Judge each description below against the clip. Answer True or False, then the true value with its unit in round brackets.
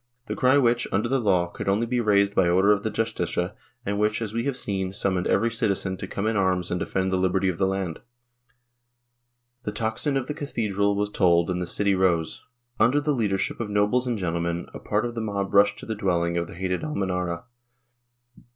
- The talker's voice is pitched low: True (100 Hz)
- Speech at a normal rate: False (215 wpm)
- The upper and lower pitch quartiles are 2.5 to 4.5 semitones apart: True (3.6 semitones)